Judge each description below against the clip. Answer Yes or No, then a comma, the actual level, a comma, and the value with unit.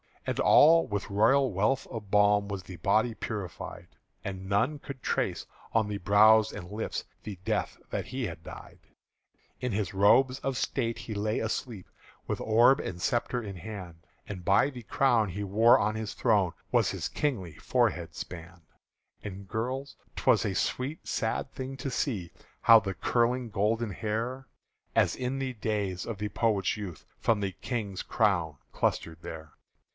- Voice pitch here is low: Yes, low, 105 Hz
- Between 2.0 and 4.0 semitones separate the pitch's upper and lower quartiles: Yes, average, 3.7 semitones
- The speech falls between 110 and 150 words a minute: No, average, 165 wpm